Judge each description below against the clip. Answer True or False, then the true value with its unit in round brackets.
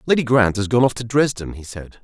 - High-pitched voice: False (115 Hz)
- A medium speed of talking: False (265 wpm)